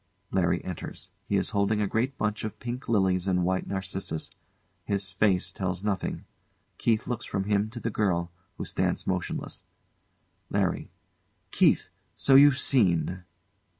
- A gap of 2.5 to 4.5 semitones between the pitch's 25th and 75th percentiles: Yes, average, 2.9 semitones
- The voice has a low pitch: Yes, low, 100 Hz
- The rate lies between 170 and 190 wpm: No, average, 145 wpm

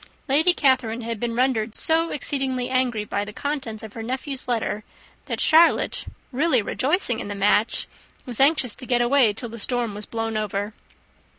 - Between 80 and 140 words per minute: No, average, 175 wpm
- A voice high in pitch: Yes, high, 240 Hz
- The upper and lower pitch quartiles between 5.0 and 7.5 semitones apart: No, average, 3.6 semitones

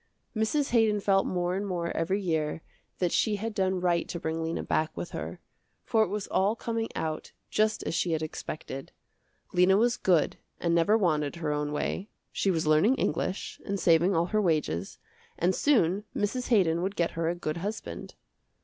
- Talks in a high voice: No, medium, 180 Hz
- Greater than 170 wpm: Yes, average, 185 wpm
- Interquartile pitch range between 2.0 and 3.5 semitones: No, average, 4.2 semitones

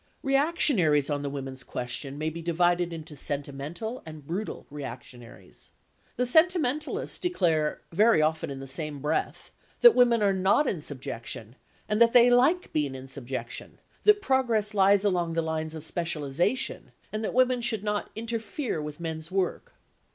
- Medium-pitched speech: Yes, medium, 170 Hz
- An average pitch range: No, wide, 7.9 semitones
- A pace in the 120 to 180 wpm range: Yes, average, 155 wpm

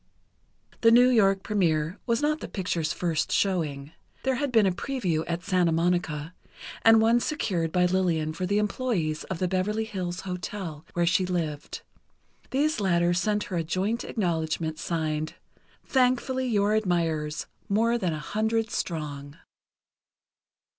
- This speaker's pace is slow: No, average, 145 wpm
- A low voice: No, medium, 185 Hz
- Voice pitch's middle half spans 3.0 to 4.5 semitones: No, average, 5.1 semitones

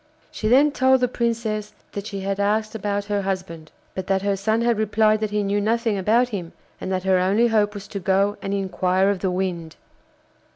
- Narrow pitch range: Yes, narrow, 2.3 semitones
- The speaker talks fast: Yes, fast, 210 wpm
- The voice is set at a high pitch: Yes, high, 205 Hz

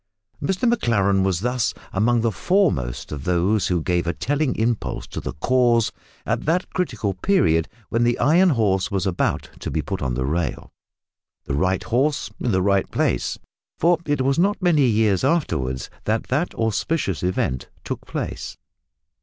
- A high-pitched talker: No, low, 110 Hz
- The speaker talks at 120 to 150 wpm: No, average, 165 wpm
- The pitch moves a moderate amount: No, wide, 7.9 semitones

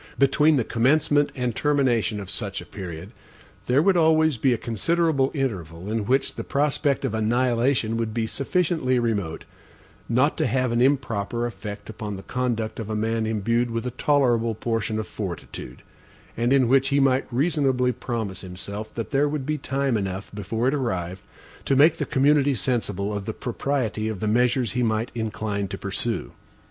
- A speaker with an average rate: Yes, average, 175 wpm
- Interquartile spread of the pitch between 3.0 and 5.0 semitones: Yes, average, 4.0 semitones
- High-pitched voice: No, low, 120 Hz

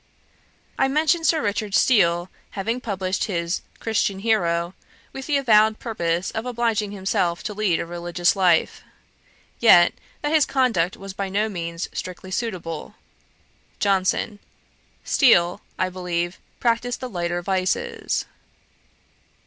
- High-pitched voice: Yes, high, 195 Hz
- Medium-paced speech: No, slow, 125 wpm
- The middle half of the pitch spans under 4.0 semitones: No, average, 4.7 semitones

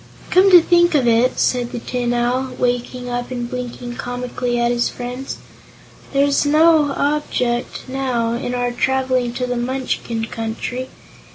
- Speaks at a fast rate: No, average, 150 wpm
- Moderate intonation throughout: No, narrow, 1.6 semitones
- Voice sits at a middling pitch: No, very high, 250 Hz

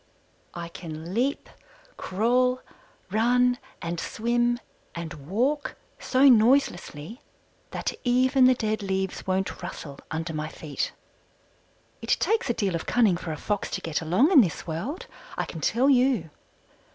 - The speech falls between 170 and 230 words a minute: No, average, 140 wpm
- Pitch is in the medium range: No, high, 215 Hz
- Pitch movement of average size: No, wide, 7.0 semitones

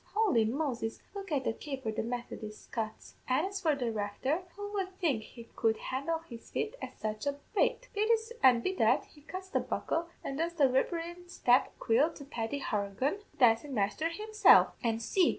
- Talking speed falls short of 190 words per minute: No, average, 195 wpm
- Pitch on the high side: Yes, very high, 280 Hz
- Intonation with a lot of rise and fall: Yes, wide, 7.4 semitones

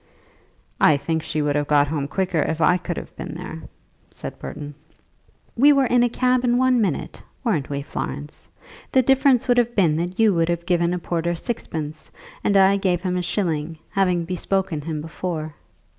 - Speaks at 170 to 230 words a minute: Yes, average, 190 wpm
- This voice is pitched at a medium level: Yes, medium, 175 Hz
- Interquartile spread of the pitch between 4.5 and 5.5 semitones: Yes, average, 4.8 semitones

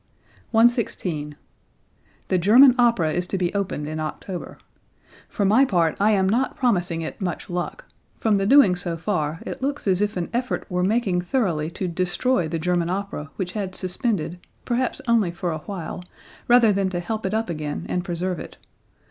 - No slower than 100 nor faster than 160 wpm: No, average, 180 wpm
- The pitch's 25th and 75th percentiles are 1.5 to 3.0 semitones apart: No, average, 4.3 semitones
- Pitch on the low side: No, medium, 185 Hz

